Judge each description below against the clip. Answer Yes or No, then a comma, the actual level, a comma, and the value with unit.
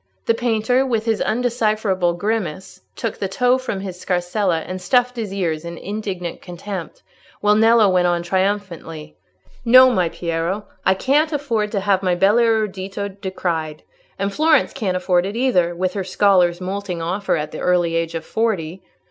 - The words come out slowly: No, average, 170 wpm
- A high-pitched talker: Yes, high, 195 Hz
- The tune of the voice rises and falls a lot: No, average, 3.8 semitones